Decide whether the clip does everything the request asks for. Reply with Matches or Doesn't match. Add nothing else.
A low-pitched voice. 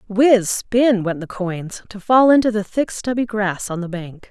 Doesn't match